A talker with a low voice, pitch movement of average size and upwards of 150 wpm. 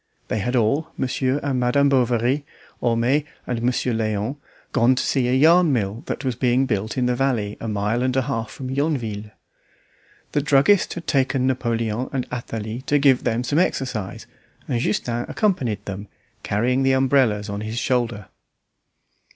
Yes: low, 125 Hz; average, 3.1 semitones; average, 165 wpm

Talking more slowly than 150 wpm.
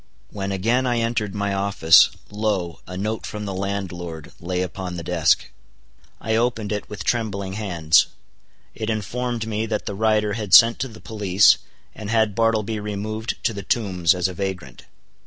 No: average, 170 wpm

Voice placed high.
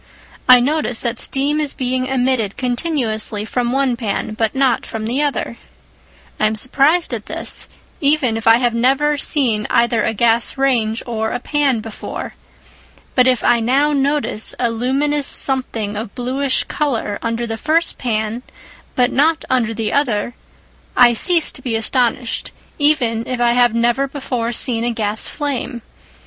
Yes: high, 245 Hz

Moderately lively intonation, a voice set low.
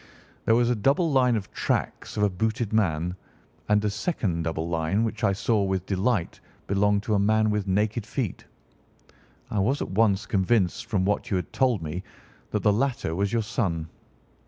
Yes: average, 3.1 semitones; low, 105 Hz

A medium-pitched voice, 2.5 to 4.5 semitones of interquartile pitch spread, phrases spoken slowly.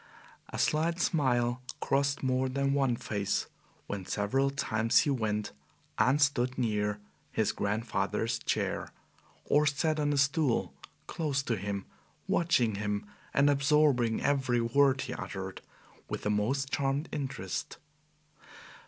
No: low, 130 Hz; average, 4.1 semitones; slow, 125 wpm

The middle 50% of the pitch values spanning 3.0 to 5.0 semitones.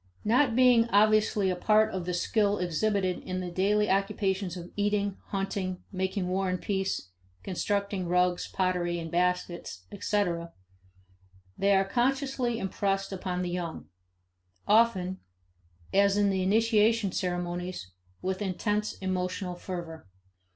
No: narrow, 2.5 semitones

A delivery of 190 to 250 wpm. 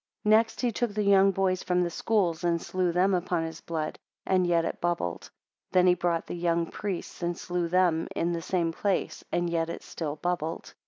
Yes: fast, 205 wpm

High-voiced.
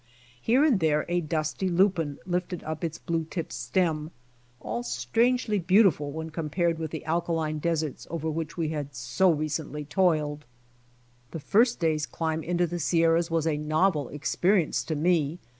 No: medium, 160 Hz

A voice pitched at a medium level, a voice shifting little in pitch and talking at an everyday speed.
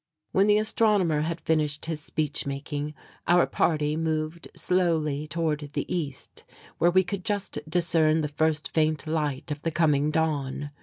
Yes: medium, 155 Hz; narrow, 2.3 semitones; average, 155 wpm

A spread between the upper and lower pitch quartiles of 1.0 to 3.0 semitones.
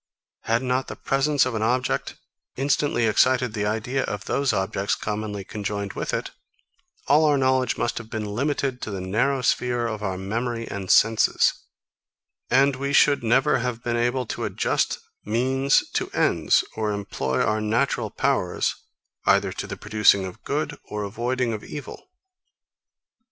No: average, 3.8 semitones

